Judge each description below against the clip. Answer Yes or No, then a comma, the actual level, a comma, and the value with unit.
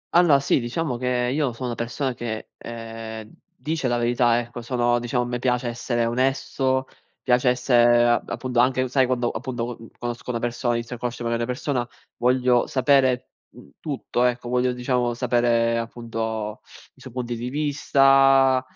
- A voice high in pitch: No, low, 125 Hz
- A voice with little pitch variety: Yes, narrow, 1.5 semitones